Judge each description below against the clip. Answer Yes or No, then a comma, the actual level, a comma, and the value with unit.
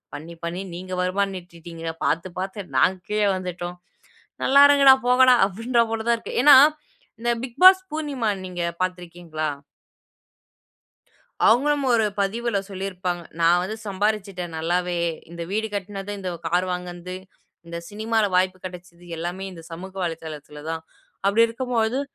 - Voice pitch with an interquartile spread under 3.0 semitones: No, average, 4.2 semitones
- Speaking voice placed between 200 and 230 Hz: No, medium, 185 Hz